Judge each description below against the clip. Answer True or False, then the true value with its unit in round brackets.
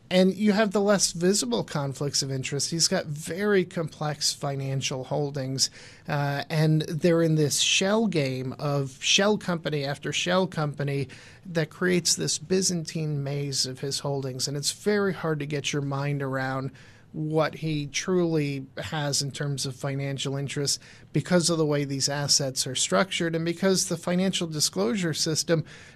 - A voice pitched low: False (150 Hz)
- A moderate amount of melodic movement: True (3.7 semitones)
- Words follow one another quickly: False (155 wpm)